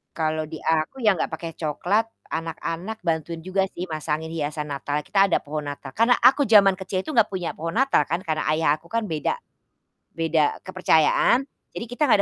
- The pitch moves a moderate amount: Yes, average, 3.9 semitones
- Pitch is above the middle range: No, medium, 165 Hz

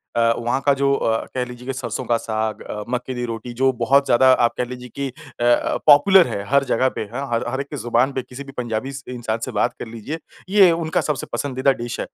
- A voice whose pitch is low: Yes, low, 125 Hz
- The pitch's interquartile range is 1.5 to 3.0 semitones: Yes, average, 2.7 semitones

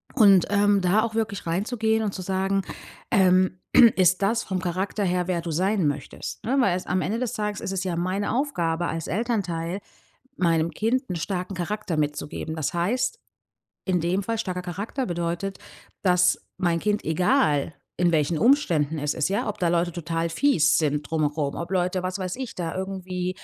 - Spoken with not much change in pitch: No, average, 3.3 semitones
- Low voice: No, medium, 185 Hz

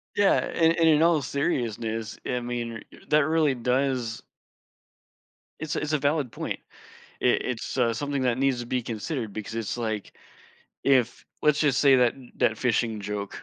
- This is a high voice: No, low, 125 Hz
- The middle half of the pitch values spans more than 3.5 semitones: Yes, average, 4.0 semitones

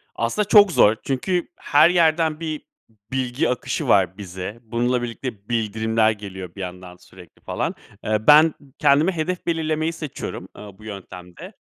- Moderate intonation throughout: No, wide, 7.3 semitones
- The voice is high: No, low, 120 Hz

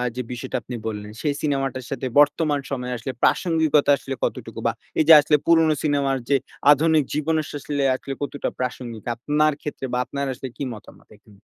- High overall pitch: No, medium, 140 Hz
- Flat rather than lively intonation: No, average, 3.0 semitones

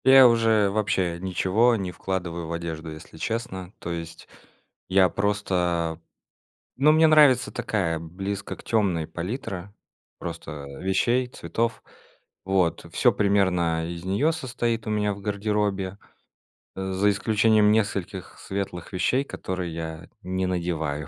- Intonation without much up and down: No, average, 3.9 semitones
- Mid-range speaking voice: No, very low, 95 Hz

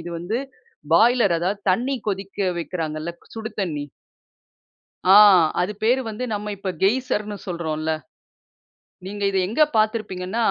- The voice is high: Yes, high, 200 Hz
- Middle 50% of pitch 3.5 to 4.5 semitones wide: Yes, average, 3.9 semitones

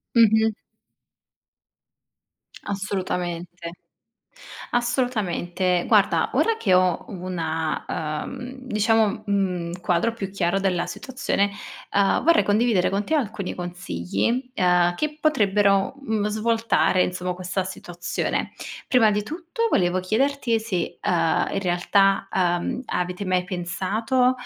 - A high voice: Yes, high, 195 Hz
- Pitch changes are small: No, average, 4.1 semitones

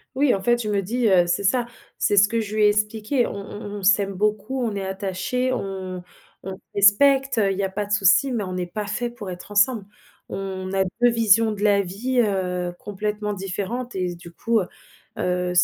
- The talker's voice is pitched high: Yes, high, 205 Hz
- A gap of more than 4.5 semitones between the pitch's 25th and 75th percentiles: No, average, 3.2 semitones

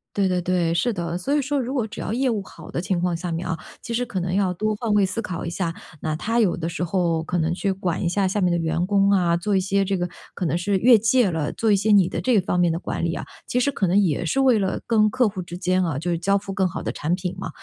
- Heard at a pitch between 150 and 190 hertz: Yes, medium, 185 Hz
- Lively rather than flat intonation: No, average, 3.4 semitones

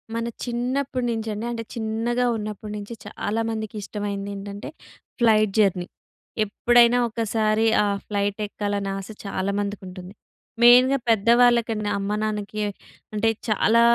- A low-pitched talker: No, high, 215 Hz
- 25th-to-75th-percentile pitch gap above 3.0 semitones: No, narrow, 2.4 semitones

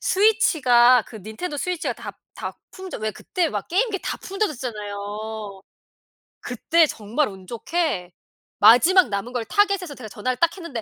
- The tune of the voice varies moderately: No, wide, 8.8 semitones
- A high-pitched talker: Yes, very high, 250 Hz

